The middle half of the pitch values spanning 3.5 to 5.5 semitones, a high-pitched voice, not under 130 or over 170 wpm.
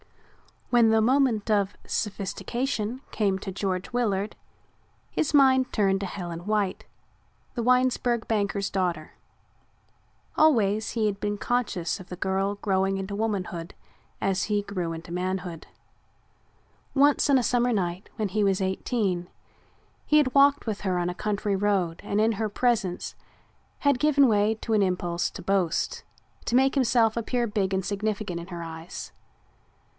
Yes: average, 3.8 semitones; high, 205 Hz; average, 150 wpm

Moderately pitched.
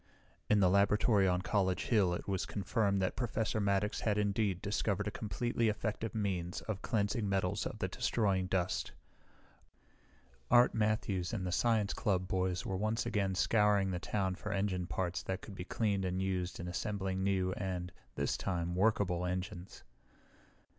No: low, 100 Hz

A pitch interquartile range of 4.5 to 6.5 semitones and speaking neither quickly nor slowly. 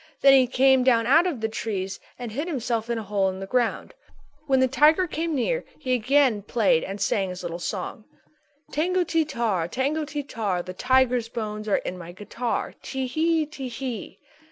Yes: average, 5.0 semitones; average, 195 wpm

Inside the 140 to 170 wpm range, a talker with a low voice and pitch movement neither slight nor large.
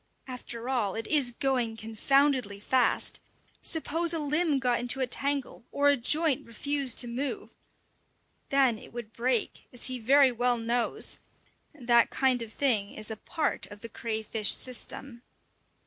No: average, 150 wpm; very high, 250 Hz; average, 3.2 semitones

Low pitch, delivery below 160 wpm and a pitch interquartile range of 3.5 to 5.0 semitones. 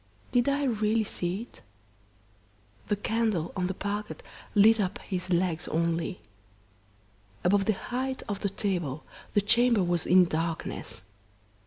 No: high, 200 Hz; slow, 135 wpm; average, 3.9 semitones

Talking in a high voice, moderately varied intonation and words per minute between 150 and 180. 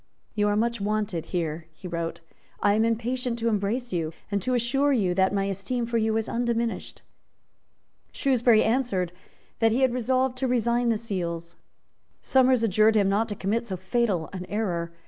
Yes: high, 220 Hz; average, 3.8 semitones; average, 175 wpm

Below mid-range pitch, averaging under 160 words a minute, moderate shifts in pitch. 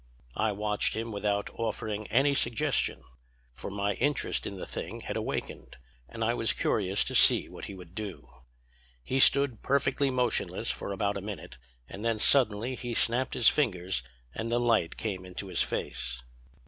No: low, 110 Hz; average, 170 wpm; average, 3.3 semitones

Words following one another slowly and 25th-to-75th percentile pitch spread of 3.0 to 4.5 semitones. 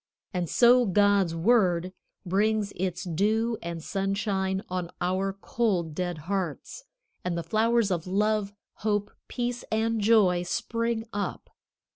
Yes: slow, 125 wpm; average, 3.4 semitones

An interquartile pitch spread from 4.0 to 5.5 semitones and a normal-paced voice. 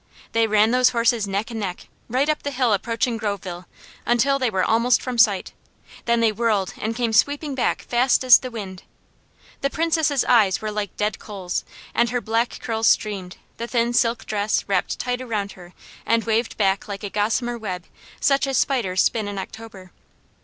No: average, 3.3 semitones; average, 185 wpm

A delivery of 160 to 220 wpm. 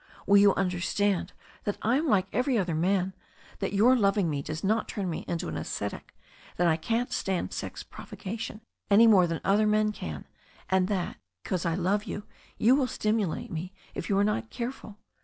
Yes: average, 190 wpm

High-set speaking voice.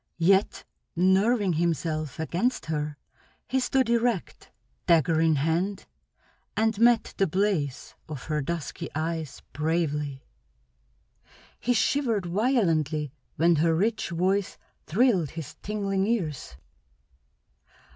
No: medium, 170 Hz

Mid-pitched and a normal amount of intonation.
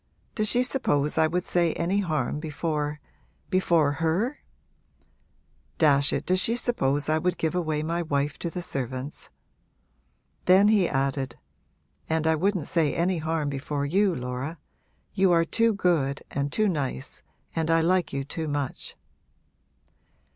Yes: medium, 160 Hz; average, 4.0 semitones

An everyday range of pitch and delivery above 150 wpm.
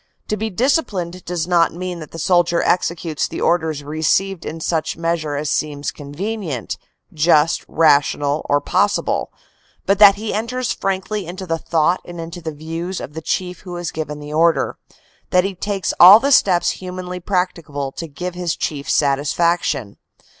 Yes: average, 3.0 semitones; average, 170 wpm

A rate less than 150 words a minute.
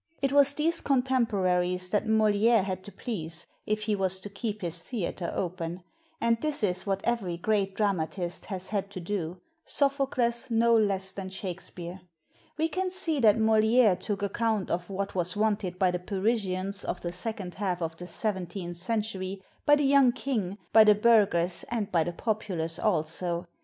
No: average, 170 wpm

